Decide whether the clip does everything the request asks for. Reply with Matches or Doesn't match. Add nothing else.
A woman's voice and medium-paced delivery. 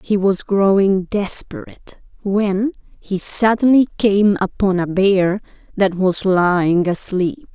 Doesn't match